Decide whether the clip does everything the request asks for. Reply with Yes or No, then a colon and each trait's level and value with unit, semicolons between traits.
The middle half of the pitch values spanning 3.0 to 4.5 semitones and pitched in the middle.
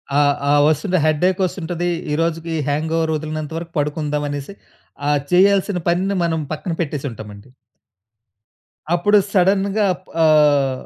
Yes: average, 3.6 semitones; medium, 165 Hz